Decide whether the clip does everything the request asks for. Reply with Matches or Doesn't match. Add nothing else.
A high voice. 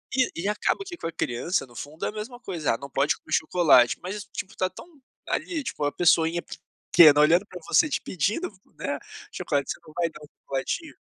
Doesn't match